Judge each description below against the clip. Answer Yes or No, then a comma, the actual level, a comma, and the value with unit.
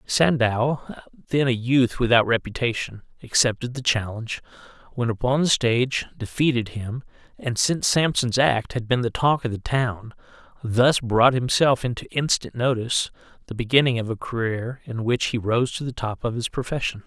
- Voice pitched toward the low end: Yes, low, 120 Hz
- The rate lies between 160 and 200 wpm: Yes, average, 165 wpm